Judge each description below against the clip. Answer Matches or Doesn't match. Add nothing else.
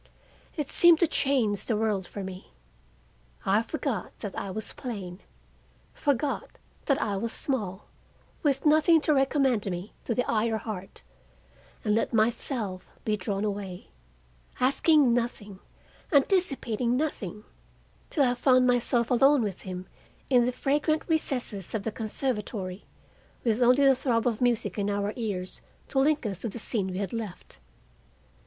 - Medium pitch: Doesn't match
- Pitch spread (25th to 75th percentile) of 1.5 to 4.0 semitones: Doesn't match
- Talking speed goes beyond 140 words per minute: Matches